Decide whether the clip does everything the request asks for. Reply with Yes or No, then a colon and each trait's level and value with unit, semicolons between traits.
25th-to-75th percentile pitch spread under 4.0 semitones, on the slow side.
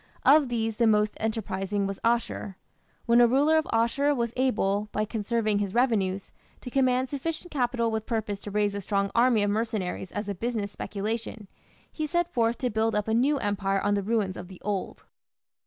No: average, 3.1 semitones; average, 190 wpm